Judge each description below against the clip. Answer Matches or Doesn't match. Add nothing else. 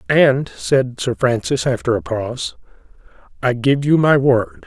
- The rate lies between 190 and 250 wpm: Doesn't match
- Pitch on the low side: Matches